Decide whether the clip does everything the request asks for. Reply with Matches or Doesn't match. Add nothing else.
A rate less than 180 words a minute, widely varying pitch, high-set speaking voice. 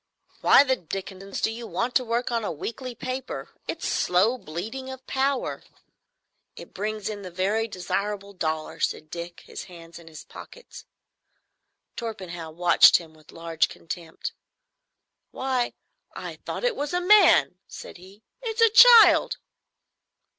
Matches